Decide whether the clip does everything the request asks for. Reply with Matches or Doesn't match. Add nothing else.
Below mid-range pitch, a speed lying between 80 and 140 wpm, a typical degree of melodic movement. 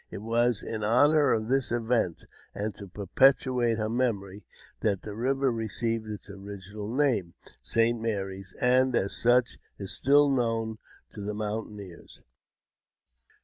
Matches